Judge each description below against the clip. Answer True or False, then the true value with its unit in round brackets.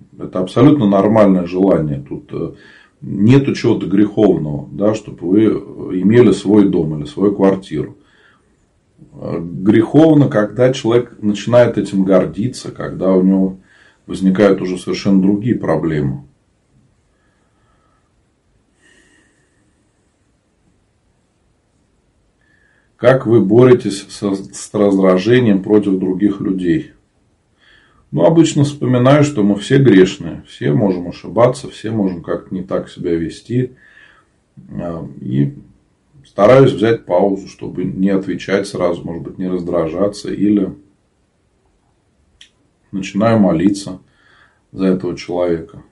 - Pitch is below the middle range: True (100 Hz)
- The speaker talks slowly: True (95 wpm)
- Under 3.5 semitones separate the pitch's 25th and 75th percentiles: True (2.8 semitones)